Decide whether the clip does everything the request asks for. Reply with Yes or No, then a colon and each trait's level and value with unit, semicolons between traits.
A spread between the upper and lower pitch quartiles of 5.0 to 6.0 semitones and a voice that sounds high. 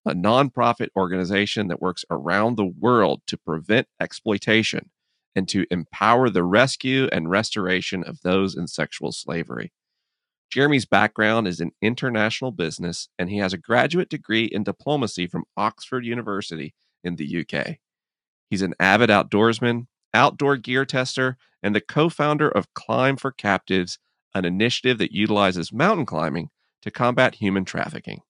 No: wide, 5.4 semitones; low, 110 Hz